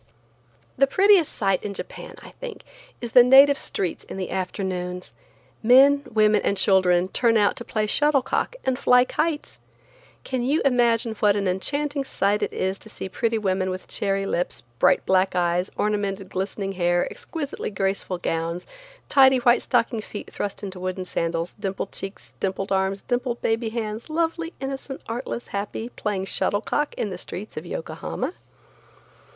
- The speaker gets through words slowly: No, average, 160 wpm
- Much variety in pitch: No, average, 4.9 semitones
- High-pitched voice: Yes, high, 210 Hz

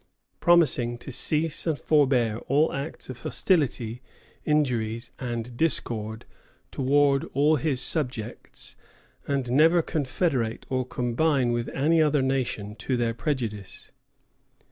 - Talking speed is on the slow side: Yes, slow, 115 wpm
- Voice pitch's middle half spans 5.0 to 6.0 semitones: No, average, 4.1 semitones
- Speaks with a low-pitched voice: Yes, low, 130 Hz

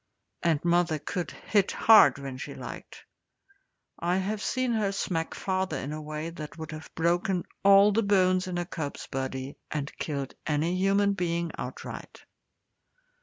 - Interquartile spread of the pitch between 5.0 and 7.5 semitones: No, average, 4.2 semitones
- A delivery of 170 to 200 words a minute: No, average, 155 wpm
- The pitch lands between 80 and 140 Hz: No, medium, 175 Hz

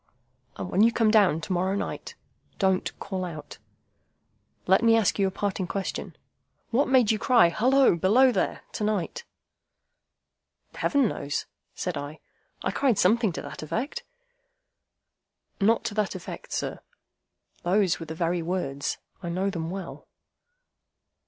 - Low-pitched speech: No, high, 195 Hz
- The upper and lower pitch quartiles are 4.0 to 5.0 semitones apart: Yes, average, 4.3 semitones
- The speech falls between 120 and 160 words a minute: Yes, average, 145 wpm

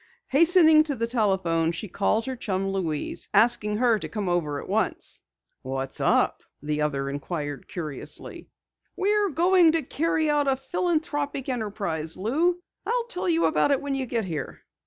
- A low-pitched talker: No, high, 230 Hz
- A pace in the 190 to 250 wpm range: No, average, 160 wpm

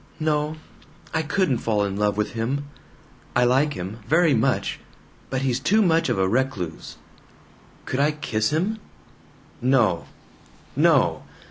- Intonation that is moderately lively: No, wide, 5.9 semitones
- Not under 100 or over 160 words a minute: Yes, slow, 135 wpm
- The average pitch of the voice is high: No, low, 130 Hz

